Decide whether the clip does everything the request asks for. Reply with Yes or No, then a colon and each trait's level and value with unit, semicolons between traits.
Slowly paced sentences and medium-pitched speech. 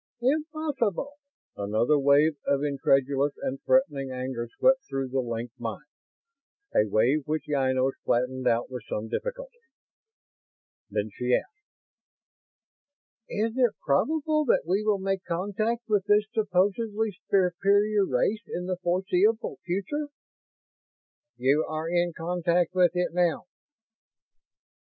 Yes: slow, 120 wpm; medium, 175 Hz